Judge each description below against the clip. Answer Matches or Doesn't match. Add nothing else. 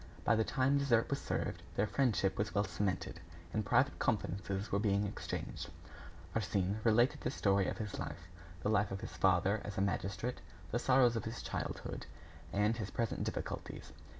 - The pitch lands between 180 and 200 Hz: Doesn't match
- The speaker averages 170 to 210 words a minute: Matches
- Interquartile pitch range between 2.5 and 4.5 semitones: Matches